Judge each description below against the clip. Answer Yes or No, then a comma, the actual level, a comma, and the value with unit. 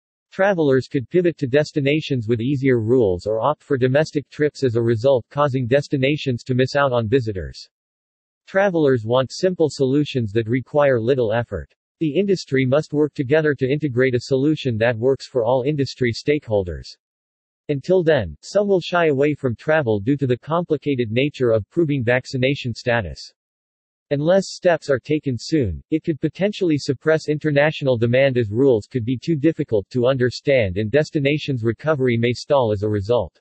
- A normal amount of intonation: Yes, average, 3.8 semitones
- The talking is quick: No, average, 160 wpm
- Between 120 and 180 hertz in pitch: Yes, low, 135 Hz